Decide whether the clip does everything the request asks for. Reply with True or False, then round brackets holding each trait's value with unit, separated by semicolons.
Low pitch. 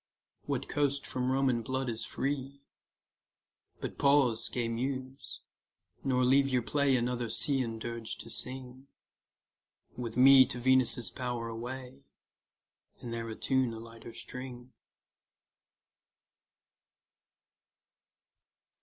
True (125 Hz)